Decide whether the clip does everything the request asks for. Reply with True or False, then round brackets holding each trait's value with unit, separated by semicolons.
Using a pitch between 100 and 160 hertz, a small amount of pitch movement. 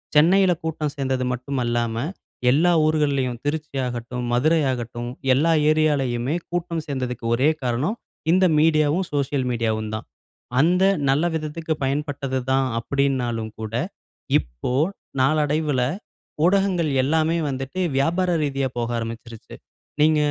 False (140 Hz; 4.1 semitones)